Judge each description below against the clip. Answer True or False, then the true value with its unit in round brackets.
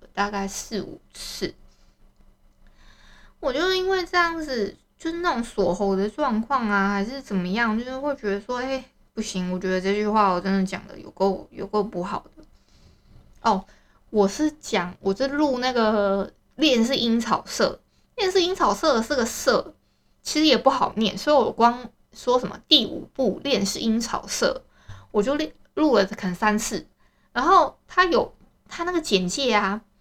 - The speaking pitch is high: True (225 Hz)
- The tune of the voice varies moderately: False (6.0 semitones)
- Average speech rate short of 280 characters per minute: True (235 characters per minute)